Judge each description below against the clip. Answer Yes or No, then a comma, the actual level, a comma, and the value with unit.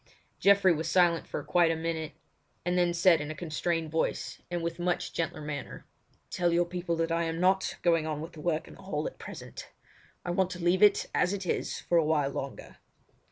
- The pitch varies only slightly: Yes, narrow, 1.7 semitones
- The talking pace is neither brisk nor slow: No, fast, 215 wpm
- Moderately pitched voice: Yes, medium, 170 Hz